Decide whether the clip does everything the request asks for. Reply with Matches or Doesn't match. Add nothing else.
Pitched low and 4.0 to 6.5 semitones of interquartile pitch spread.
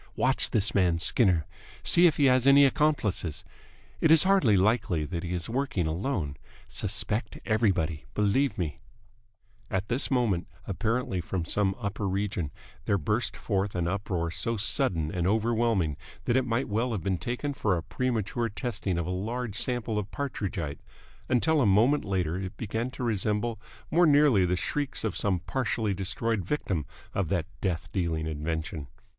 Matches